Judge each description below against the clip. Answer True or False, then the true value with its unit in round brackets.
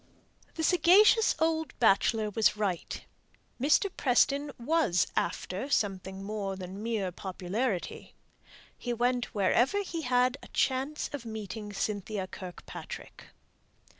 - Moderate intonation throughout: False (6.2 semitones)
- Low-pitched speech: False (225 Hz)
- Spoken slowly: True (110 wpm)